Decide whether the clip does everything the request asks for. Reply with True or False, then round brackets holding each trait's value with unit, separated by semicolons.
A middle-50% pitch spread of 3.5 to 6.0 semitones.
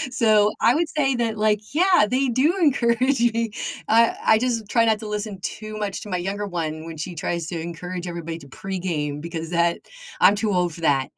True (5.2 semitones)